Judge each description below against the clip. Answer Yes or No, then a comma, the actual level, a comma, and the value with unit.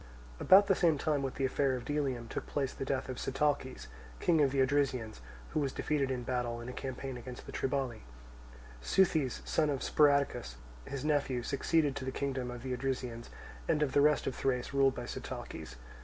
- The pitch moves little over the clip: Yes, narrow, 2.3 semitones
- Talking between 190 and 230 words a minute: Yes, average, 195 wpm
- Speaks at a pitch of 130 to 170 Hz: Yes, low, 135 Hz